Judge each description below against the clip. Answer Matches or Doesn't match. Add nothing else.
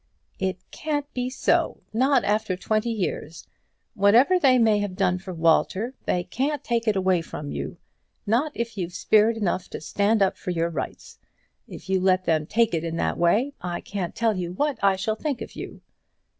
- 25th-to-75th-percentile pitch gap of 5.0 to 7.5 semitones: Doesn't match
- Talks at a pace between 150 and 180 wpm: Doesn't match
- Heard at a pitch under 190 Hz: Doesn't match